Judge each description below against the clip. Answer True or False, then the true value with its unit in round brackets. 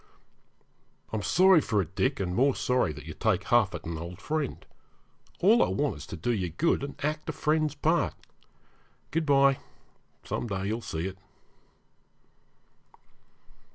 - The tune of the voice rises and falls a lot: True (7.9 semitones)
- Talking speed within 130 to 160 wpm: True (155 wpm)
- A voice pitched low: True (125 Hz)